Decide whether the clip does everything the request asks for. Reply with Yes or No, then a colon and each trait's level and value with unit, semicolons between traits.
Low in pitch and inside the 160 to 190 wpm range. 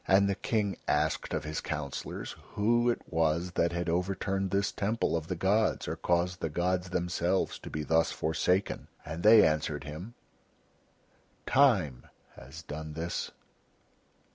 No: very low, 90 Hz; average, 145 wpm